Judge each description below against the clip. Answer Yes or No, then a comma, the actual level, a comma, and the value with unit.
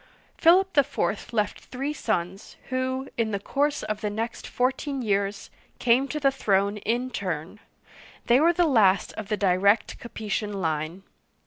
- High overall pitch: Yes, high, 220 Hz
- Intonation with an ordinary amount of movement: Yes, average, 4.9 semitones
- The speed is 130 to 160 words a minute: Yes, average, 150 wpm